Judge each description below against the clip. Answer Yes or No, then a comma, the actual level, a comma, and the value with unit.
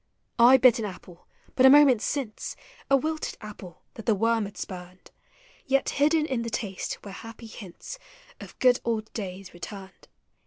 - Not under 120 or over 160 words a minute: No, average, 180 wpm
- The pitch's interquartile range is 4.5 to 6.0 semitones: Yes, average, 5.1 semitones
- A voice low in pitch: No, high, 225 Hz